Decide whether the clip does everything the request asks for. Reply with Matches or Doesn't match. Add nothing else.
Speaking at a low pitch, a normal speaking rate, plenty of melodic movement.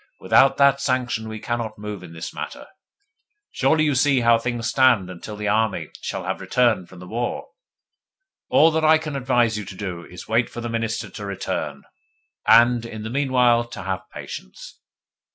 Doesn't match